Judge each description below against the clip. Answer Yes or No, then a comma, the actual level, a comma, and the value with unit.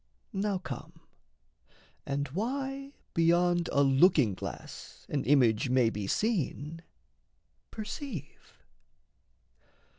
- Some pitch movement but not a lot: No, wide, 7.0 semitones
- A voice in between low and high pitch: Yes, medium, 165 Hz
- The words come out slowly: Yes, slow, 85 wpm